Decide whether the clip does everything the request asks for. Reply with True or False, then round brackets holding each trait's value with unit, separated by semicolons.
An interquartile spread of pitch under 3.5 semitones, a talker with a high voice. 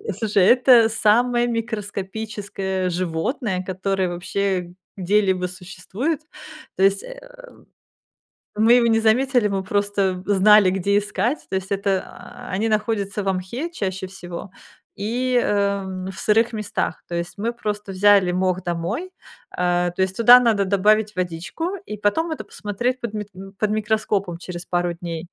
True (3.1 semitones; 200 Hz)